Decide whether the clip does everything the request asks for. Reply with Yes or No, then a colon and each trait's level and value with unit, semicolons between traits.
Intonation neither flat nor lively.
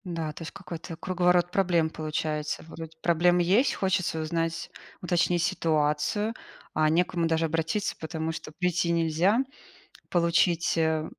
No: narrow, 1.9 semitones